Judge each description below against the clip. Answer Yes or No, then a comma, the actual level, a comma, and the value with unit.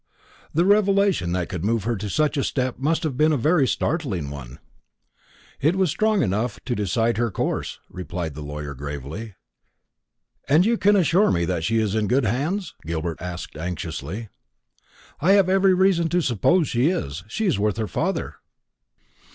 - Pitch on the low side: Yes, low, 115 Hz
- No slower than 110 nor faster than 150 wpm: No, average, 170 wpm